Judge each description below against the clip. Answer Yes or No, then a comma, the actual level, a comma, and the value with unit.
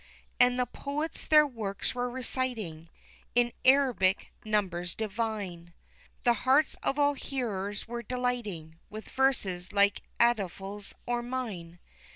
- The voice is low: No, high, 225 Hz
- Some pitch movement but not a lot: Yes, average, 4.8 semitones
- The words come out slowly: Yes, slow, 115 wpm